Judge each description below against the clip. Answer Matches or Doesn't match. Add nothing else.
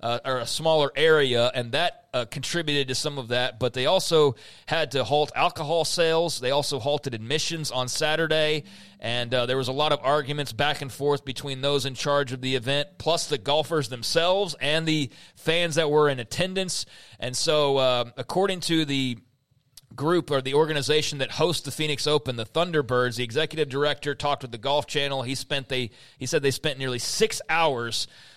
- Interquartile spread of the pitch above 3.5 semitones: Doesn't match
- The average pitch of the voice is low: Doesn't match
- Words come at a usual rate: Matches